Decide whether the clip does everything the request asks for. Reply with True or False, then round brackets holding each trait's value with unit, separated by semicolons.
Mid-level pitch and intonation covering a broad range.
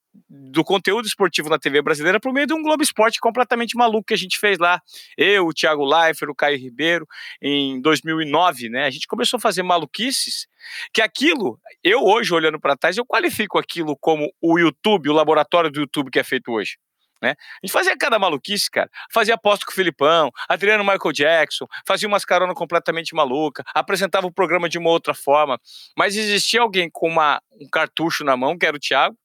True (180 Hz; 6.1 semitones)